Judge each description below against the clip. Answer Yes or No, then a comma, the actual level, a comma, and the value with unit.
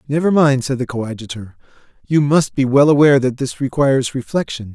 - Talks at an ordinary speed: Yes, average, 175 wpm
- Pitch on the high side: No, low, 135 Hz